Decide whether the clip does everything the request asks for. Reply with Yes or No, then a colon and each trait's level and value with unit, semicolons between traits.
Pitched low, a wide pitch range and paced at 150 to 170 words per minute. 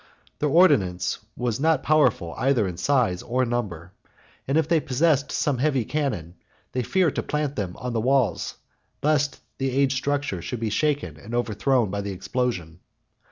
Yes: low, 125 Hz; wide, 6.1 semitones; average, 165 wpm